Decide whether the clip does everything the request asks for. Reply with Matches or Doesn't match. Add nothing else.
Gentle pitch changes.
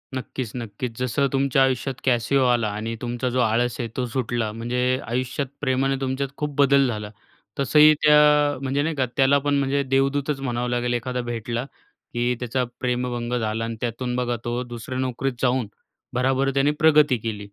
Matches